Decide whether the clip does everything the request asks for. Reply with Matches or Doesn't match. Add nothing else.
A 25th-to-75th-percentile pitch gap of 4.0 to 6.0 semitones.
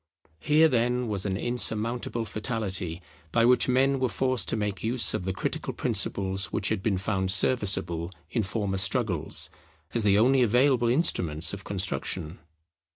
Matches